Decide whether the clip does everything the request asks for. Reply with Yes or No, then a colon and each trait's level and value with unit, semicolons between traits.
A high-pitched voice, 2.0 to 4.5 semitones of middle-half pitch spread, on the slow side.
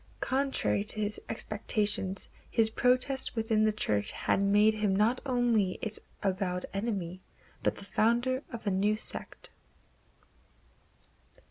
Yes: high, 215 Hz; average, 2.8 semitones; slow, 125 wpm